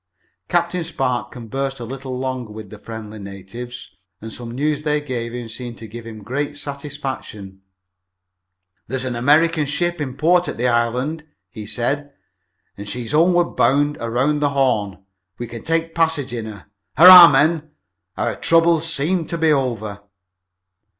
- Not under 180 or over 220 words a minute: No, average, 155 wpm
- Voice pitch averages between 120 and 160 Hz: Yes, low, 135 Hz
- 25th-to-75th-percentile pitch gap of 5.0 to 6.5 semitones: No, average, 4.6 semitones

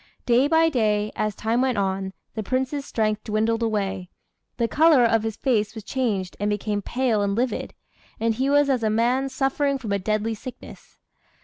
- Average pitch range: Yes, average, 3.8 semitones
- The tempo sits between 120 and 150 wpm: No, average, 185 wpm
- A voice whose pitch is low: No, high, 225 Hz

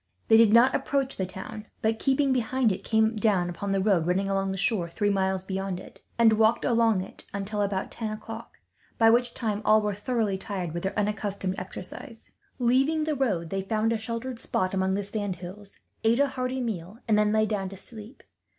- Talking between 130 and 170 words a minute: No, fast, 205 wpm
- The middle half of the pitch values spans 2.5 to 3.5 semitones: Yes, average, 3.1 semitones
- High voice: Yes, high, 210 Hz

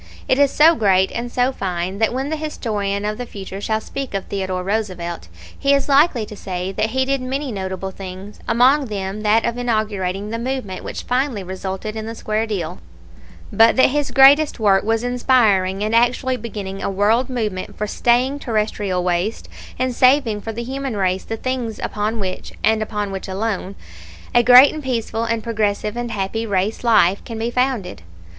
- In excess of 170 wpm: Yes, average, 185 wpm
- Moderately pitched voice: No, high, 220 Hz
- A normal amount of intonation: Yes, average, 4.1 semitones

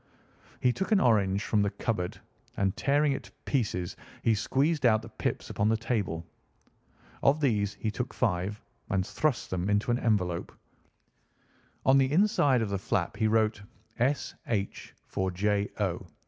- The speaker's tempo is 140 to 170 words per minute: Yes, average, 160 wpm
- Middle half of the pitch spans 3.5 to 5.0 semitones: Yes, average, 4.4 semitones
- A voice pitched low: Yes, low, 110 Hz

